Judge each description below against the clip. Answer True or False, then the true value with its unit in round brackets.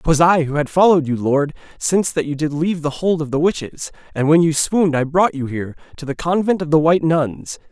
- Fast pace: True (250 wpm)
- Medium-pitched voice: True (155 Hz)